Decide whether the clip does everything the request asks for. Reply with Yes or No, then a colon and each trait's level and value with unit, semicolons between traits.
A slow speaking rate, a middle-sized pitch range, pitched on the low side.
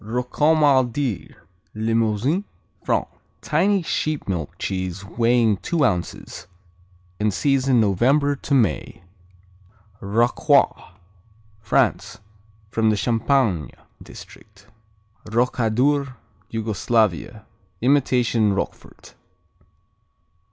Yes: slow, 75 wpm; average, 4.4 semitones; low, 115 Hz